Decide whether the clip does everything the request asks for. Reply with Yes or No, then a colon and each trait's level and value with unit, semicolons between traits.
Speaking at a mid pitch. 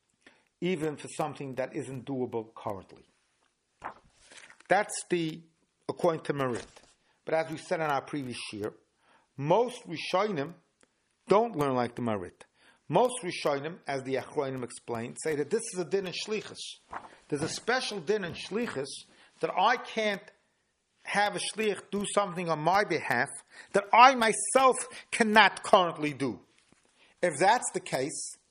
Yes: medium, 170 Hz